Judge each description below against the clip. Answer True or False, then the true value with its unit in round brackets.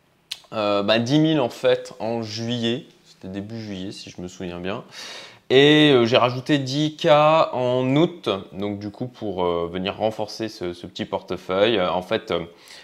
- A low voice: True (110 Hz)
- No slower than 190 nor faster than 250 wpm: False (180 wpm)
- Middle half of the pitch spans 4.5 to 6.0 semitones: True (5.1 semitones)